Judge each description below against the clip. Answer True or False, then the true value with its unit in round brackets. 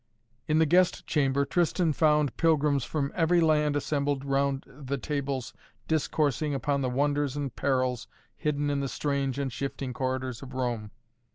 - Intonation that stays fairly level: True (2.0 semitones)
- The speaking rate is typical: True (155 wpm)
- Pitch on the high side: False (140 Hz)